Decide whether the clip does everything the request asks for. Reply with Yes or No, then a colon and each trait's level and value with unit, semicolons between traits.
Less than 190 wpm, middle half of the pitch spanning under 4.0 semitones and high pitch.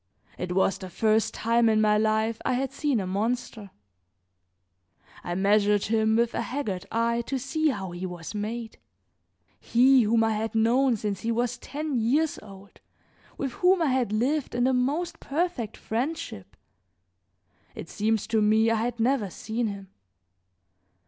Yes: average, 160 wpm; average, 3.3 semitones; high, 225 Hz